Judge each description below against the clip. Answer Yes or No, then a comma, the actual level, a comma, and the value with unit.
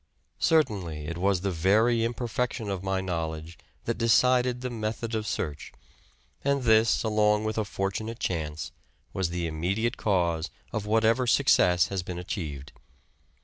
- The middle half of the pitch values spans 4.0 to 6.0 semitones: Yes, average, 4.7 semitones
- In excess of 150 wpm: No, average, 145 wpm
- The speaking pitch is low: Yes, low, 100 Hz